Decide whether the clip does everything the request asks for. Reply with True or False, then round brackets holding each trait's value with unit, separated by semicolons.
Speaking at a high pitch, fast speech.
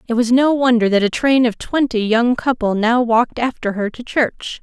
True (240 Hz; 220 wpm)